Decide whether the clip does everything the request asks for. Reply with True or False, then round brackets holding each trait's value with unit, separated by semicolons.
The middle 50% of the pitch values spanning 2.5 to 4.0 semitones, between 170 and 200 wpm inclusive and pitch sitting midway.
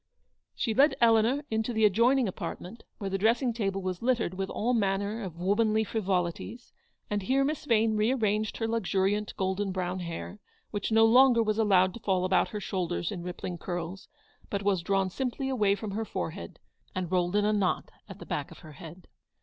False (3.3 semitones; 190 wpm; 205 Hz)